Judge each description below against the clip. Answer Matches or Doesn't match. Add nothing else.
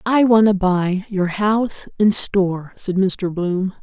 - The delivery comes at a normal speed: Matches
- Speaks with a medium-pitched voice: Doesn't match